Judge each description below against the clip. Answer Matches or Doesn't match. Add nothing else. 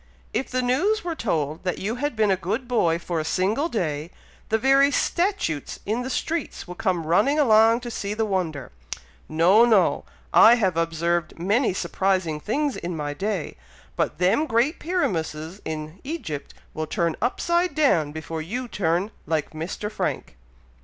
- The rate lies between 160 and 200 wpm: Matches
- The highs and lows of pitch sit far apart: Matches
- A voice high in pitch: Matches